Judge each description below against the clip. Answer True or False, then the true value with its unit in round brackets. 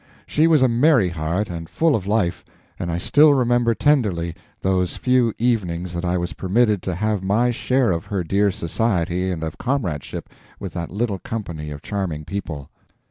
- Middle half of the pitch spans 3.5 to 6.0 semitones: True (5.6 semitones)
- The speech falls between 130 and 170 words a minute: False (180 wpm)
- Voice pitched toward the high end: False (95 Hz)